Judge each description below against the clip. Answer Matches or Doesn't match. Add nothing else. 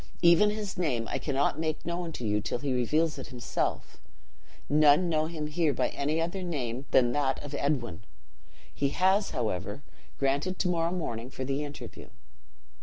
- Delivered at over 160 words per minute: Matches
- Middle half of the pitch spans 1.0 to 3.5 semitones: Doesn't match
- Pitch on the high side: Doesn't match